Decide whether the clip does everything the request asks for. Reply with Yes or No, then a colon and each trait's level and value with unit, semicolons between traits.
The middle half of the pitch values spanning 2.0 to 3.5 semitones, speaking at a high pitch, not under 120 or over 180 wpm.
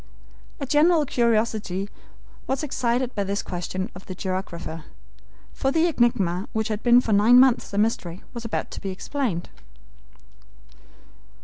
No: average, 4.9 semitones; high, 220 Hz; average, 140 wpm